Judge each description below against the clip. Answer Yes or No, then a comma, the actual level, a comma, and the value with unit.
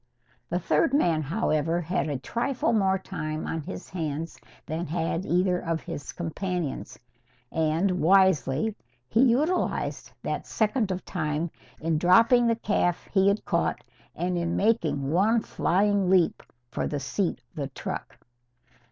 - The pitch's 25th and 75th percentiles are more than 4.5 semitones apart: No, average, 4.2 semitones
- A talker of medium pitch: Yes, medium, 175 Hz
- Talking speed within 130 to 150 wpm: Yes, average, 145 wpm